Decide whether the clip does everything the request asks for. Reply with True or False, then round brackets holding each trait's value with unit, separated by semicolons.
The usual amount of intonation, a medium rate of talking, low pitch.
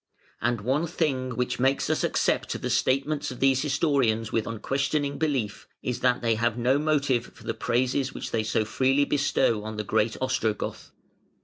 True (3.5 semitones; 175 wpm; 130 Hz)